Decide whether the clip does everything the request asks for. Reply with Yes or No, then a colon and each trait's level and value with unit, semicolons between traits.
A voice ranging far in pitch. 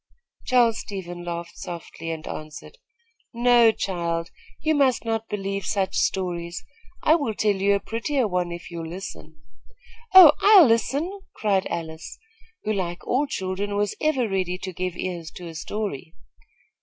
No: average, 4.9 semitones